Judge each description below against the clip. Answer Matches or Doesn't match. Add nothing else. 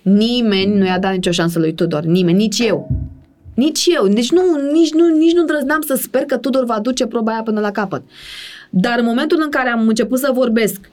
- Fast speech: Matches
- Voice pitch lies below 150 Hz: Doesn't match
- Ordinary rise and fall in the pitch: Doesn't match